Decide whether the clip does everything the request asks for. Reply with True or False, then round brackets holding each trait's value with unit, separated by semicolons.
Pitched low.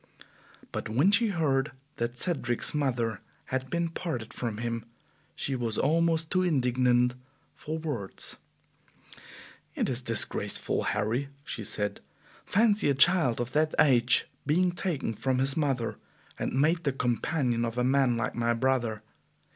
True (130 Hz)